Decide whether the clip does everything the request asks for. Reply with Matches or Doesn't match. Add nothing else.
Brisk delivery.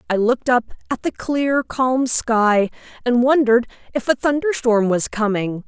Doesn't match